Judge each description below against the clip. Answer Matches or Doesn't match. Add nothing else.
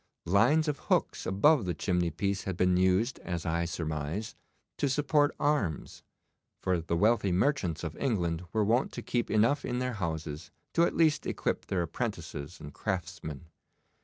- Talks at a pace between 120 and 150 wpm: Doesn't match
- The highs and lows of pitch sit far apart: Matches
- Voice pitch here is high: Doesn't match